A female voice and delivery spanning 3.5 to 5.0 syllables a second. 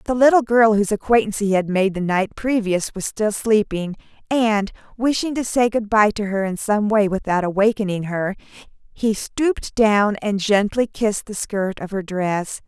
Yes: female; 4.8 syllables/s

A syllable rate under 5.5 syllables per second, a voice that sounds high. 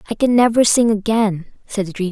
No: 5.7 syllables/s; high, 215 Hz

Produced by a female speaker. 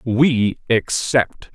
No: male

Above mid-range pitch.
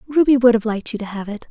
Yes: high, 230 Hz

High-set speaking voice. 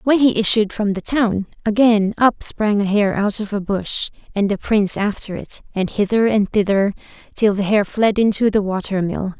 Yes: high, 205 Hz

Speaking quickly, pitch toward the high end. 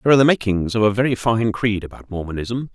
No: fast, 240 wpm; low, 110 Hz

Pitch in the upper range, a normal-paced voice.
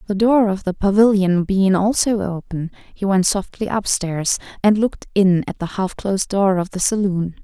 Yes: high, 195 Hz; average, 185 wpm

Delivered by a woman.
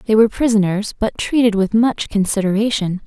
Yes: female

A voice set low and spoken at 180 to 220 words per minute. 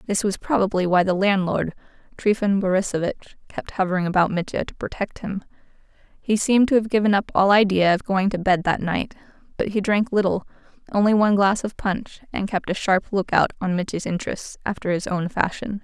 No: high, 195 Hz; average, 195 wpm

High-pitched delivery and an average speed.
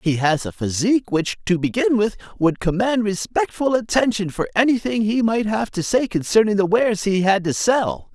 Yes: high, 210 Hz; average, 190 wpm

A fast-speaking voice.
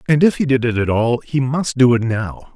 Yes: fast, 280 wpm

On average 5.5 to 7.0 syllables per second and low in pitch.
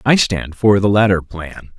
No: 4.3 syllables/s; very low, 95 Hz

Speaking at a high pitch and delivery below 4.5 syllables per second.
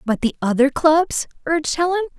No: very high, 305 Hz; 5.3 syllables/s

